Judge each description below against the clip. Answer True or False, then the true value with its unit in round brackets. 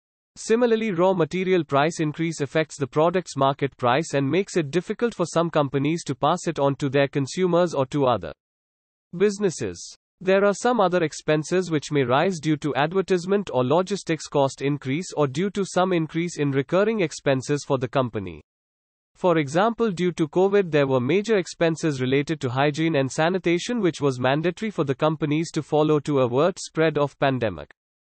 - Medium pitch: True (155 Hz)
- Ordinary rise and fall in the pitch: True (4.5 semitones)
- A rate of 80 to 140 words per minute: False (175 wpm)